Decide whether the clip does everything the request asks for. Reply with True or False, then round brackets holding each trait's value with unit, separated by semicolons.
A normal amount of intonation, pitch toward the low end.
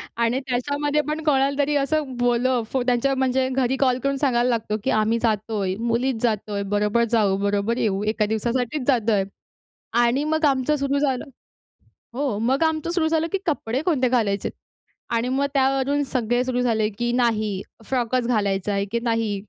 False (3.7 semitones; 245 Hz)